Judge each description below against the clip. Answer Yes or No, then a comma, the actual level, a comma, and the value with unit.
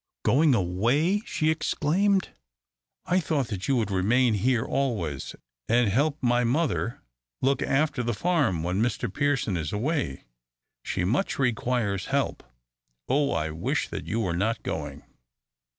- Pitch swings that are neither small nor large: No, wide, 6.8 semitones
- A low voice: Yes, low, 120 Hz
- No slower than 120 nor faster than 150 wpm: Yes, average, 140 wpm